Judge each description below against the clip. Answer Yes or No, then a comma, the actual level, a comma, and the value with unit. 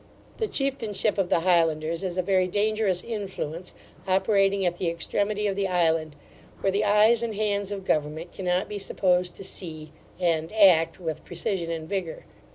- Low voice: No, medium, 185 Hz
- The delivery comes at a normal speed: Yes, average, 165 wpm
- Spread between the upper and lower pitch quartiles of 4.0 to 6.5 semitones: No, average, 3.3 semitones